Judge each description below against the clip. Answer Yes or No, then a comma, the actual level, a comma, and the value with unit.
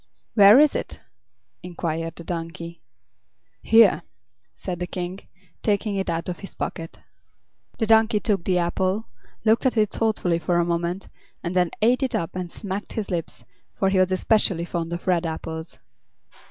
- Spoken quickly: No, average, 165 wpm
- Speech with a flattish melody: No, average, 3.6 semitones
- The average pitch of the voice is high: No, medium, 180 Hz